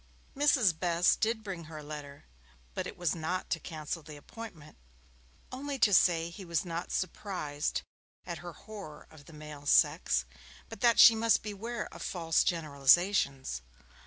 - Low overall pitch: No, medium, 170 Hz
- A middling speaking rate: Yes, average, 160 wpm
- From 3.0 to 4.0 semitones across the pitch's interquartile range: No, average, 5.2 semitones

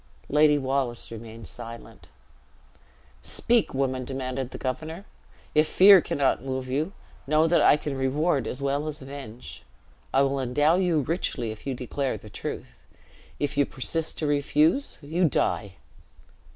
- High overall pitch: No, medium, 140 Hz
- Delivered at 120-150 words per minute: Yes, average, 145 wpm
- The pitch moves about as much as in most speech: Yes, average, 3.1 semitones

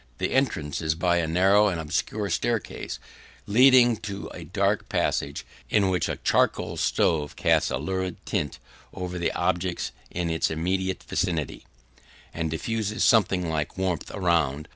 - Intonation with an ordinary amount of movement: Yes, average, 3.5 semitones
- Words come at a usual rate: Yes, average, 145 wpm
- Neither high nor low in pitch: No, very low, 90 Hz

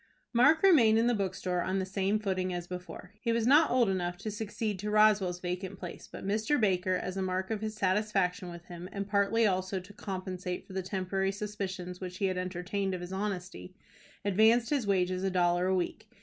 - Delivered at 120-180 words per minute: No, fast, 205 wpm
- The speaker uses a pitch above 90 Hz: Yes, high, 190 Hz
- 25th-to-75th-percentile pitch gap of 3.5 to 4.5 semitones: No, narrow, 2.5 semitones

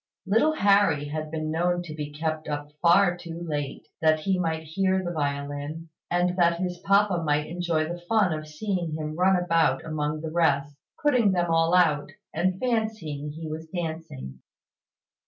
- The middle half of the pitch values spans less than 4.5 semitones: Yes, average, 2.8 semitones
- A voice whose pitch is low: No, medium, 165 Hz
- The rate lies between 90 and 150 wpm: No, average, 170 wpm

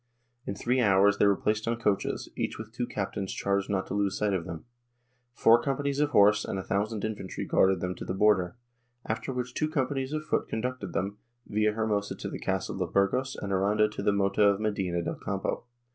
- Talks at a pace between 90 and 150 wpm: No, fast, 205 wpm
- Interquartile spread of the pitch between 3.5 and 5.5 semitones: No, average, 3.1 semitones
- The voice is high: No, low, 105 Hz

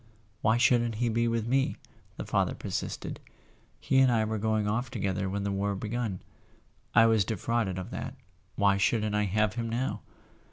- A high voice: No, low, 110 Hz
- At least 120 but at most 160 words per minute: No, average, 175 wpm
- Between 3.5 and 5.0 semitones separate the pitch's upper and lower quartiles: No, narrow, 2.6 semitones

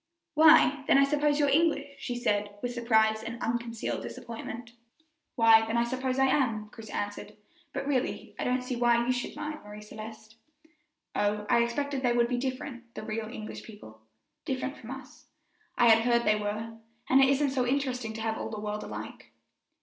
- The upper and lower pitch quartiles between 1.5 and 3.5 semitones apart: Yes, average, 3.2 semitones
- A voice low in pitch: No, high, 240 Hz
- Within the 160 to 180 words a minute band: No, average, 190 wpm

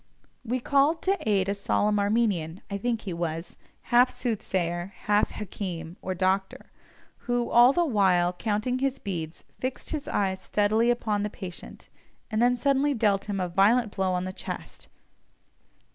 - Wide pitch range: No, average, 4.4 semitones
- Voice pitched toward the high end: Yes, high, 205 Hz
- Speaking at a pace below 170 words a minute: Yes, average, 160 wpm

